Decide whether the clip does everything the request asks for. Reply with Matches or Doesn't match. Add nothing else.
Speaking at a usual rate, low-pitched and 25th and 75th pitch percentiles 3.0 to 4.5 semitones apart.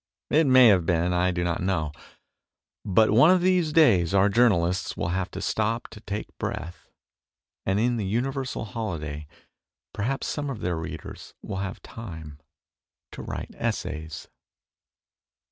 Doesn't match